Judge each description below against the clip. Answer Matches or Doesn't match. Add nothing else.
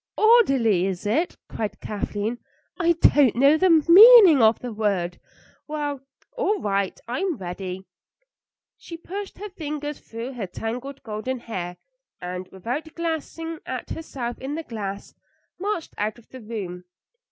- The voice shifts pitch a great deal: Matches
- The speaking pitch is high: Matches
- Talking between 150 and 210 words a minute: Doesn't match